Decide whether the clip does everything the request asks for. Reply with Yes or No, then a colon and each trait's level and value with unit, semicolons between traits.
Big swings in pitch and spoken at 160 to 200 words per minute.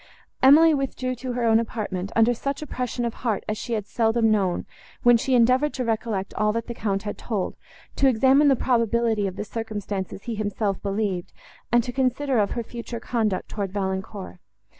No: average, 3.2 semitones; average, 185 wpm